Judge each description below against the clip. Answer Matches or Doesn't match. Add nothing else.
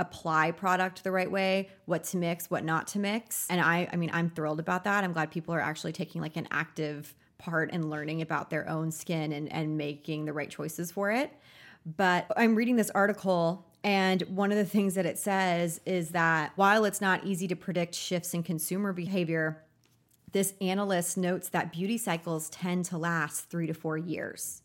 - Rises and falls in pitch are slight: Doesn't match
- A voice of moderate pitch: Matches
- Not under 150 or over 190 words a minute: Doesn't match